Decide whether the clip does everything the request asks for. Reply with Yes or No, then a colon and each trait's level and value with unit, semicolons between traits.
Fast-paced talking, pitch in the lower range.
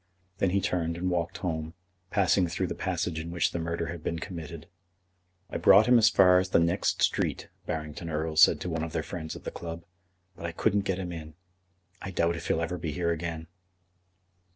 Yes: fast, 210 wpm; very low, 85 Hz